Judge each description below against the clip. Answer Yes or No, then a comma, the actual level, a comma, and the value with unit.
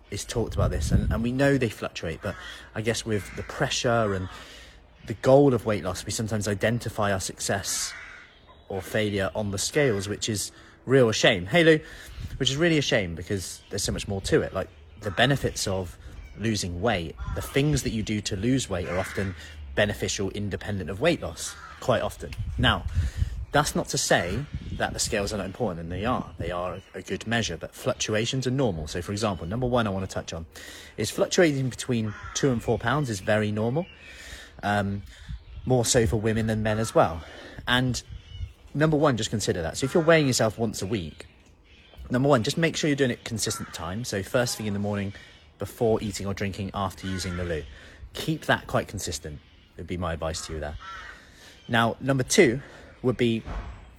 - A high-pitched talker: No, low, 105 Hz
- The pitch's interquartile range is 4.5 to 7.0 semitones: Yes, average, 4.8 semitones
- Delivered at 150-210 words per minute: Yes, average, 200 wpm